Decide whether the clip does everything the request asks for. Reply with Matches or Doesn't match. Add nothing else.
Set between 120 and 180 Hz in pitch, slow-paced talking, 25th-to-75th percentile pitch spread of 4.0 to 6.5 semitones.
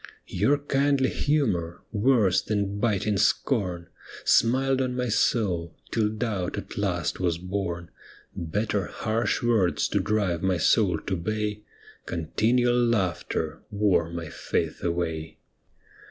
Doesn't match